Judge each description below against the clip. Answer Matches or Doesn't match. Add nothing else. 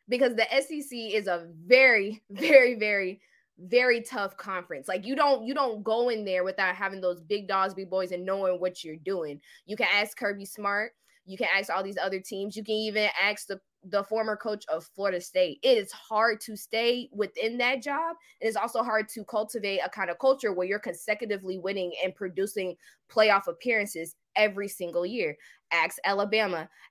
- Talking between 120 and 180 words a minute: Doesn't match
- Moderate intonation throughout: Matches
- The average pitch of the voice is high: Matches